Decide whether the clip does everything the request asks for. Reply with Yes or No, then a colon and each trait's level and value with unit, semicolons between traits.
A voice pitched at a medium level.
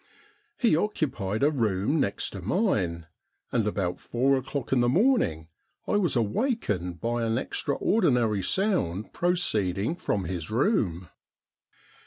No: low, 115 Hz